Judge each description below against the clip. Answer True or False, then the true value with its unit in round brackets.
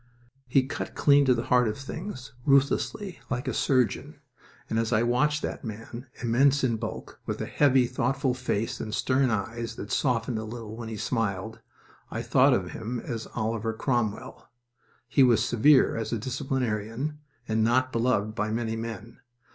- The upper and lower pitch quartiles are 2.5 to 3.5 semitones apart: True (2.8 semitones)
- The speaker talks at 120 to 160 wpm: False (170 wpm)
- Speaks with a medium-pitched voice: False (120 Hz)